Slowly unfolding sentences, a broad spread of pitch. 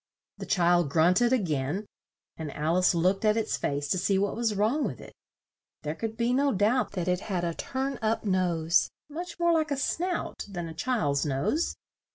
No: fast, 205 wpm; wide, 6.7 semitones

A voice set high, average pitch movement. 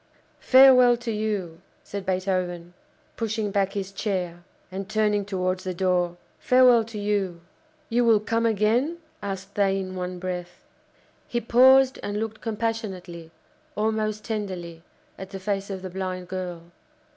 Yes: high, 200 Hz; average, 3.1 semitones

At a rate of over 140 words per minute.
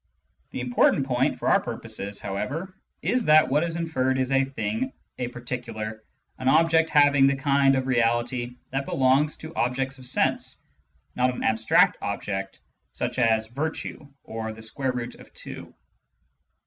Yes: average, 160 wpm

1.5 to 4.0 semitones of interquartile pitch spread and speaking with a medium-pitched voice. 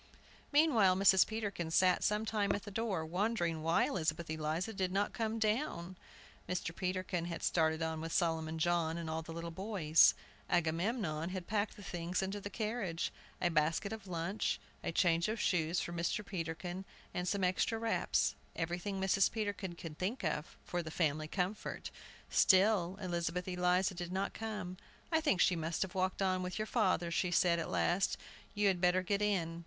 Yes: average, 3.3 semitones; medium, 180 Hz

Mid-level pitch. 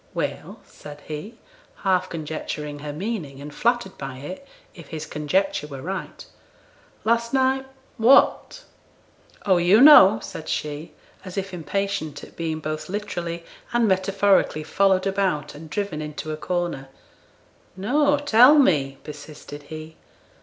Yes: medium, 175 Hz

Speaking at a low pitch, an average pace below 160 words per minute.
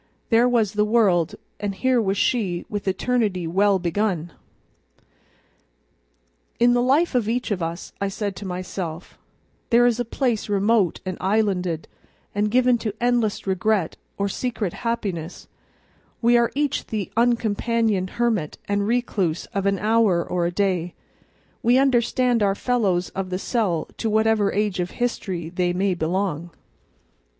No: high, 205 Hz; average, 145 wpm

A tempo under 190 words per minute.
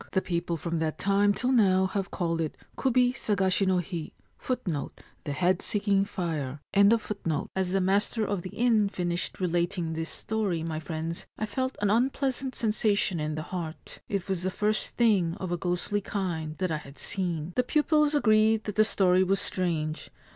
Yes: average, 170 wpm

